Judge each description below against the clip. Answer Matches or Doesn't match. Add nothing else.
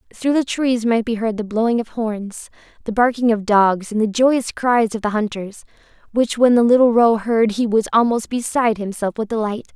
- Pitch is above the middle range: Matches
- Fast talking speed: Matches